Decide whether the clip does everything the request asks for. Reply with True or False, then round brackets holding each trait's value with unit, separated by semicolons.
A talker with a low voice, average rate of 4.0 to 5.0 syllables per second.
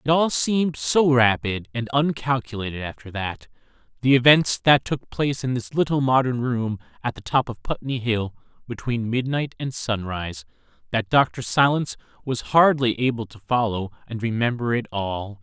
True (120 Hz; 4.9 syllables/s)